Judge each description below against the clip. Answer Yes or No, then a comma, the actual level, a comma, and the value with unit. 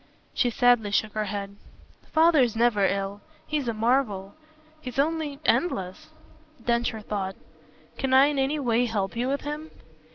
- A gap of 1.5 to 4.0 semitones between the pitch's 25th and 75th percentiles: No, average, 5.2 semitones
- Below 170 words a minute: Yes, average, 150 wpm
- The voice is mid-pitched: No, high, 240 Hz